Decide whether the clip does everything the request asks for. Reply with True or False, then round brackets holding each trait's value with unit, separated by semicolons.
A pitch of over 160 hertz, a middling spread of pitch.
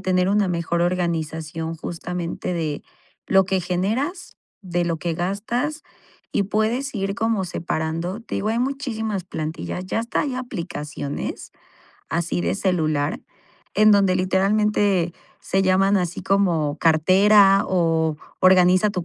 True (185 Hz; 3.6 semitones)